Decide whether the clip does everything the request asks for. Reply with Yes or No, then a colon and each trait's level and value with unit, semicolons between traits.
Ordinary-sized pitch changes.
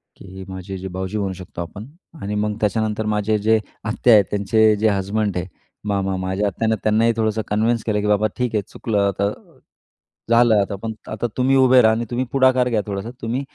No: narrow, 2.2 semitones